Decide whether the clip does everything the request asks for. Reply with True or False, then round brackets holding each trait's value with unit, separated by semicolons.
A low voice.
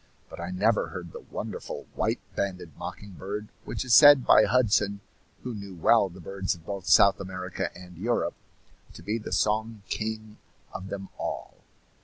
True (100 Hz)